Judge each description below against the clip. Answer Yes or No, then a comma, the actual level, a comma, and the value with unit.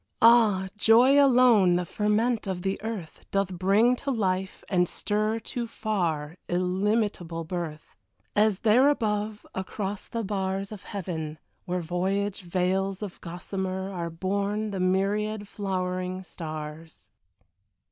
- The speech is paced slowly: Yes, slow, 125 wpm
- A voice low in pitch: No, high, 195 Hz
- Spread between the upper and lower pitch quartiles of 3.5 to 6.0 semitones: No, average, 2.8 semitones